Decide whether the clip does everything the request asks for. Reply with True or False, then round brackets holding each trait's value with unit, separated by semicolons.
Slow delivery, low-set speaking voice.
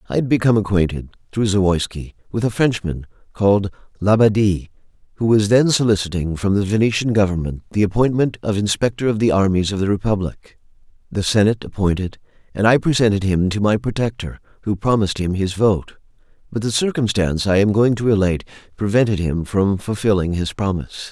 False (165 wpm; 100 Hz)